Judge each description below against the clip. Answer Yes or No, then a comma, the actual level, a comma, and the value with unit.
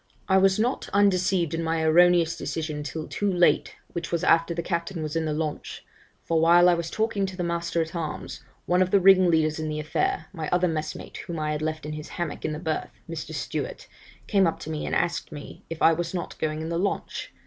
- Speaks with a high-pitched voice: No, medium, 170 Hz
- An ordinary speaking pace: No, fast, 230 wpm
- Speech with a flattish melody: Yes, narrow, 2.2 semitones